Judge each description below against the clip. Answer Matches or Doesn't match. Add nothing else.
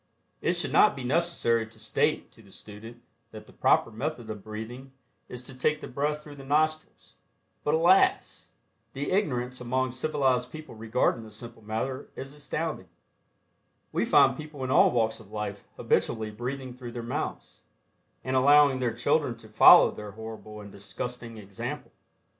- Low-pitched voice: Matches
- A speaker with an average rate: Matches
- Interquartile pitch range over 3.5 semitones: Matches